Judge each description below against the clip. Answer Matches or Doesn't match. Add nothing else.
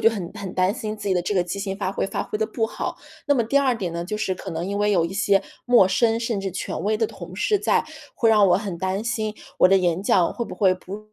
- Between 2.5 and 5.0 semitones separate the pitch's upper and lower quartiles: Matches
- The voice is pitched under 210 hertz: Matches